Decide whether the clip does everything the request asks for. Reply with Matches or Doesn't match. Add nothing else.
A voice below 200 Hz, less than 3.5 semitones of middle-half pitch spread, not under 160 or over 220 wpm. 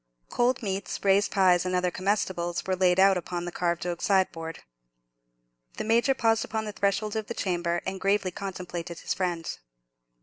Matches